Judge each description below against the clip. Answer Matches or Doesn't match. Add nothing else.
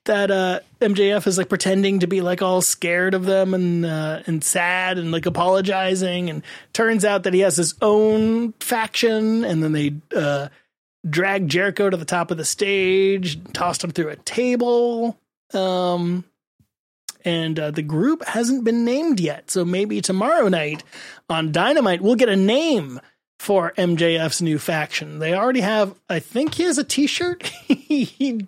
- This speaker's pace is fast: Doesn't match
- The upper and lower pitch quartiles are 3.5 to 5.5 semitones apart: Matches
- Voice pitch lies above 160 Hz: Matches